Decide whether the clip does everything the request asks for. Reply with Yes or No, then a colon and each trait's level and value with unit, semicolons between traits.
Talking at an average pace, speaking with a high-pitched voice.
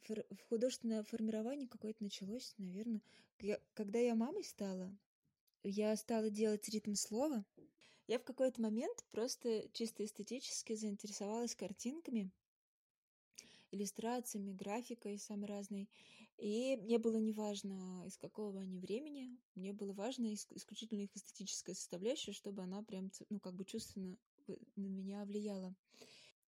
Yes: average, 125 wpm; high, 215 Hz